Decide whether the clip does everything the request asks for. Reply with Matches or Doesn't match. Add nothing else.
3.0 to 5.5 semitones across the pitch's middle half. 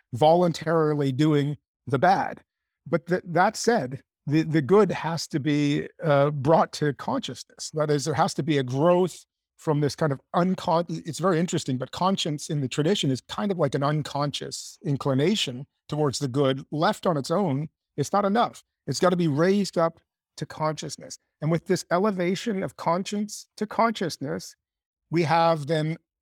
Matches